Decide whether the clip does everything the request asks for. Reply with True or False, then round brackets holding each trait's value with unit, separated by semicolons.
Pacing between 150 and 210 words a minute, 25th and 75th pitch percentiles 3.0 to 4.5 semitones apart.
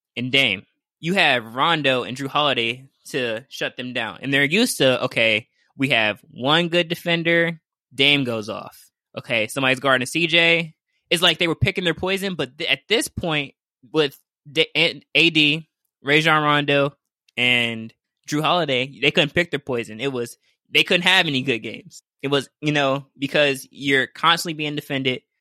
True (170 wpm; 3.7 semitones)